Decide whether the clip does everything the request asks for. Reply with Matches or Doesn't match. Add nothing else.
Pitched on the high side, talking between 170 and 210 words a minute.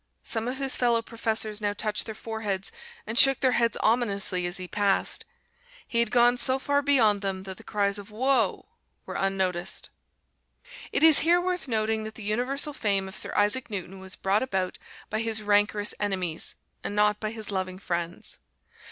Matches